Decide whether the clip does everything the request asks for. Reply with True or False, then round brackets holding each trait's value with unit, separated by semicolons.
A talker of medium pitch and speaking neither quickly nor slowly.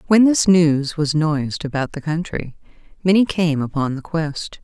True (160 Hz; 170 wpm)